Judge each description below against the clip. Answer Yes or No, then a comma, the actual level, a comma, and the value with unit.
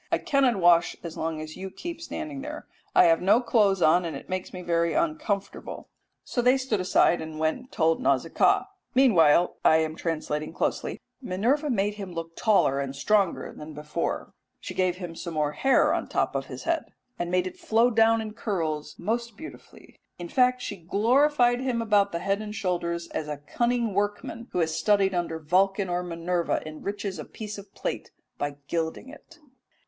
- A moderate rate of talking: Yes, average, 190 wpm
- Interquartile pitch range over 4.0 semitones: Yes, wide, 5.6 semitones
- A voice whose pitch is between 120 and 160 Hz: No, high, 190 Hz